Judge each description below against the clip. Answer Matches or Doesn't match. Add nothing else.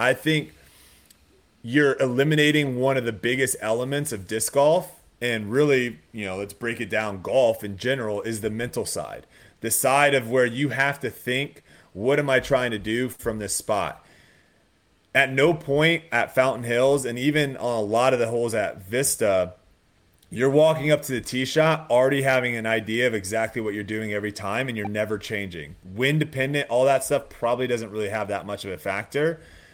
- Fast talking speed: Doesn't match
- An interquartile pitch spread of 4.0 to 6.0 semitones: Matches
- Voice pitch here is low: Matches